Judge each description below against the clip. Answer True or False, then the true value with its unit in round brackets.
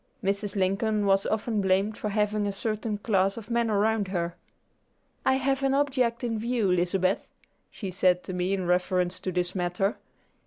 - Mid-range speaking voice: False (200 Hz)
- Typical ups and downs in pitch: True (3.0 semitones)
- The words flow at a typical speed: True (170 wpm)